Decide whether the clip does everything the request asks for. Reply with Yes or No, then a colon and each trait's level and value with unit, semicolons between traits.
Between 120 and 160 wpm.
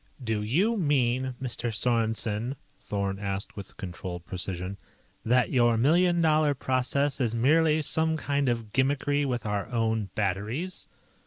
Yes: slow, 135 wpm